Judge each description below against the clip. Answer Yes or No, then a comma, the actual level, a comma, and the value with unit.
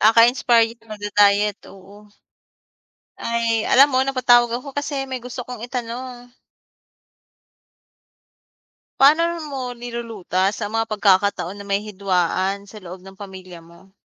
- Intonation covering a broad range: No, average, 3.7 semitones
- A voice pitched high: Yes, high, 225 Hz